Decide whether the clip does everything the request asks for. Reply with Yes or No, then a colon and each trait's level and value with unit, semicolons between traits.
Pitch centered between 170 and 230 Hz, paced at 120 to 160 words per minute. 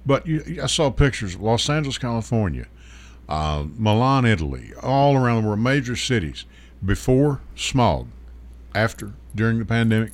No: low, 115 Hz; average, 140 wpm